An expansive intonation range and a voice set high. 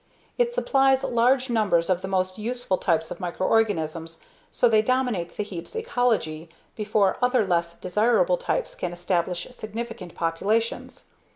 Yes: wide, 5.9 semitones; high, 210 Hz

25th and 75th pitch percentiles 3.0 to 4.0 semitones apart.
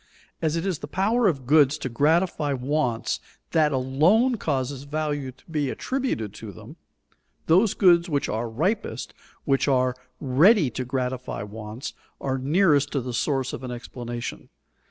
No: average, 4.4 semitones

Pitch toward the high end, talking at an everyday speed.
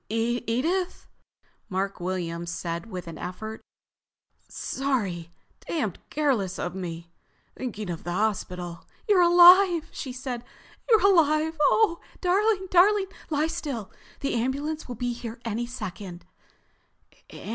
No: high, 240 Hz; slow, 115 wpm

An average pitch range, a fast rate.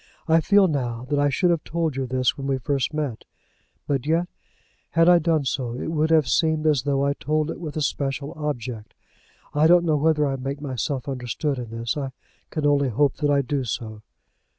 Yes: average, 3.1 semitones; fast, 210 wpm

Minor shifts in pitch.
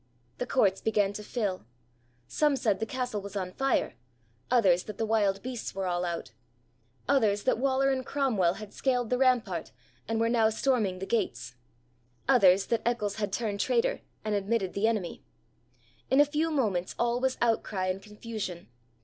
No: average, 4.3 semitones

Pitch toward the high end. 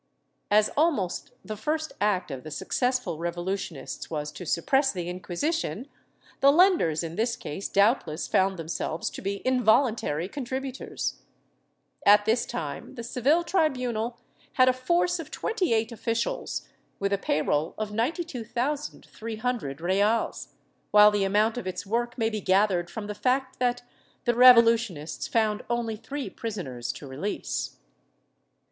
Yes: high, 220 Hz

